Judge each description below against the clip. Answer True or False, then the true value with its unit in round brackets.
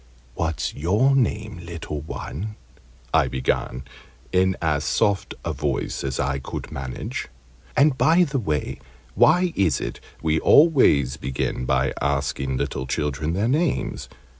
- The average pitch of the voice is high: False (80 Hz)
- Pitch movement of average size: False (8.1 semitones)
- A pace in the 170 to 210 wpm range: False (135 wpm)